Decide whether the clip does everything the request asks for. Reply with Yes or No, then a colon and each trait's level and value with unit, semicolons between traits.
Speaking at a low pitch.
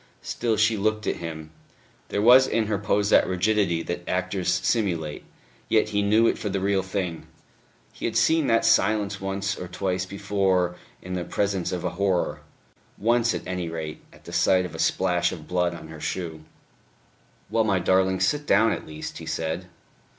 Yes: very low, 95 Hz